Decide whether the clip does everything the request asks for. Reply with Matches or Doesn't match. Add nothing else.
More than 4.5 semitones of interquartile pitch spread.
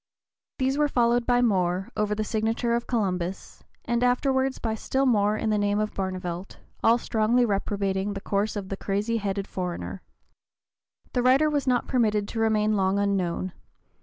Doesn't match